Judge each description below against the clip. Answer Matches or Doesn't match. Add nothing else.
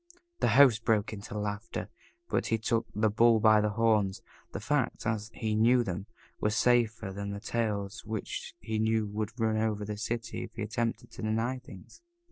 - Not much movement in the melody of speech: Matches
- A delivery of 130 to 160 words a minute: Doesn't match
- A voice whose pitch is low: Matches